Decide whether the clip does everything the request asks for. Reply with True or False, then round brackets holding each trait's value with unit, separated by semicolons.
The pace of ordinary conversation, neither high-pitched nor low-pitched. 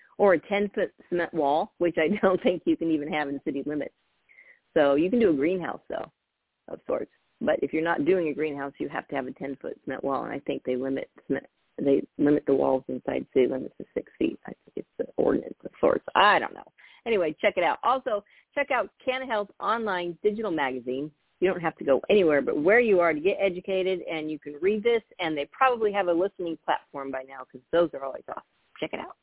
False (235 wpm; 170 Hz)